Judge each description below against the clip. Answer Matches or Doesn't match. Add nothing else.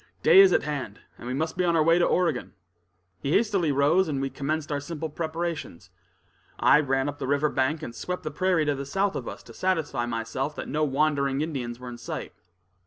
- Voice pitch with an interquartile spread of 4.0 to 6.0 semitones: Doesn't match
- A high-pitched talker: Doesn't match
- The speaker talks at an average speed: Doesn't match